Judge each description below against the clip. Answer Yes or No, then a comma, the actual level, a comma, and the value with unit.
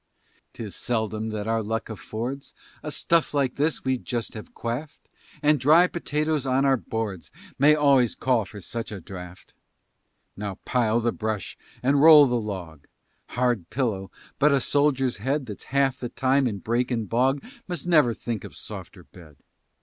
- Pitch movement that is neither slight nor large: Yes, average, 4.2 semitones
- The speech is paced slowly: No, average, 165 wpm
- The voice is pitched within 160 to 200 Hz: No, low, 125 Hz